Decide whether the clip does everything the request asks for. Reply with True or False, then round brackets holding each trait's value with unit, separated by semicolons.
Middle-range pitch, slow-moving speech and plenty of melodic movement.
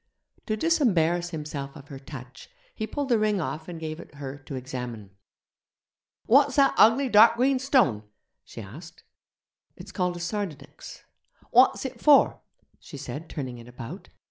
False (165 Hz; 155 wpm; 8.5 semitones)